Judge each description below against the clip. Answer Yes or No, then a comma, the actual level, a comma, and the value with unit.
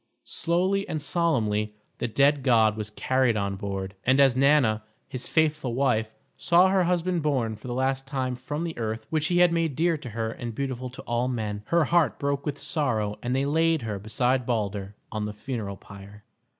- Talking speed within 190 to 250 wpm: Yes, average, 195 wpm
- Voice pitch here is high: No, low, 130 Hz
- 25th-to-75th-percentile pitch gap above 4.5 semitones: Yes, wide, 5.6 semitones